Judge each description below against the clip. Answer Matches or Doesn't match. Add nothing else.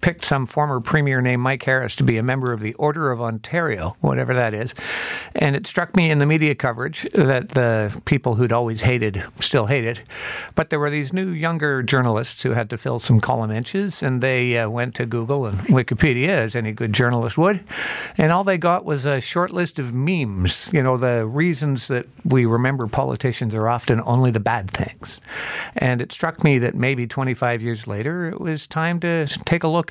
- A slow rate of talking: Doesn't match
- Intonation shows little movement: Doesn't match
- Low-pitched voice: Matches